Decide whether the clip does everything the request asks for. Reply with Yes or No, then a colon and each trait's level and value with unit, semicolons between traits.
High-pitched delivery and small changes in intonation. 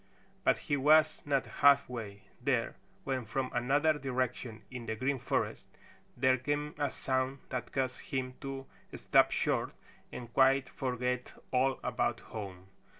No: low, 130 Hz; narrow, 1.9 semitones